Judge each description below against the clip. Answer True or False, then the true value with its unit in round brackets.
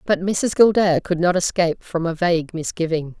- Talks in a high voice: False (175 Hz)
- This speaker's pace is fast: False (170 wpm)